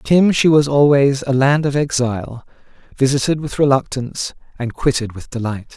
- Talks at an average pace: Yes, average, 165 wpm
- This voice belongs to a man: Yes, male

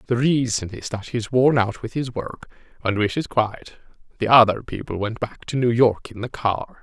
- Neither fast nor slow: No, fast, 210 wpm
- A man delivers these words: Yes, male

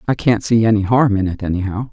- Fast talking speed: Yes, fast, 250 wpm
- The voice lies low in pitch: Yes, low, 105 Hz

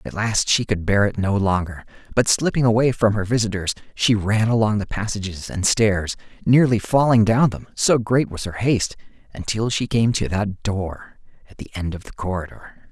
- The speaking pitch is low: Yes, low, 105 Hz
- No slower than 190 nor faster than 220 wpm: Yes, average, 195 wpm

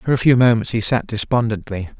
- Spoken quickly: Yes, fast, 210 wpm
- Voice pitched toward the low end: Yes, low, 115 Hz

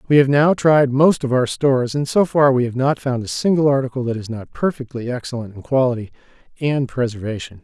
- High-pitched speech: No, low, 130 Hz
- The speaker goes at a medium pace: No, fast, 210 wpm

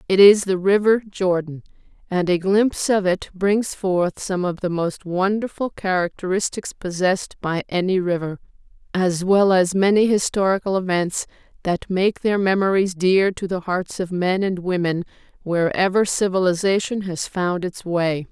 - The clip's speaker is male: No, female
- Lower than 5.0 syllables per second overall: Yes, 4.6 syllables/s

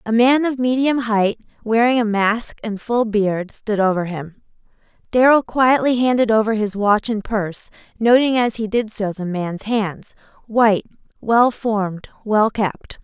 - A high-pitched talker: Yes, high, 220 Hz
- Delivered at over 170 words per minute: No, average, 160 wpm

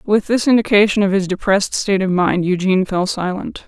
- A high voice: Yes, high, 195 Hz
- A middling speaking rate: Yes, average, 195 wpm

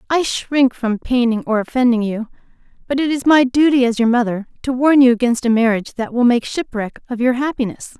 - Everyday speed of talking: No, fast, 210 wpm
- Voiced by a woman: Yes, female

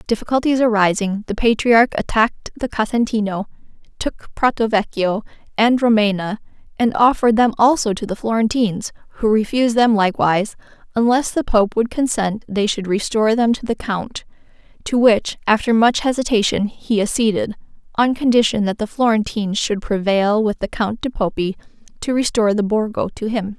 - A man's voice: No, female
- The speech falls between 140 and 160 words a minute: Yes, average, 155 wpm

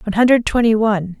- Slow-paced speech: No, average, 200 wpm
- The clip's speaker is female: Yes, female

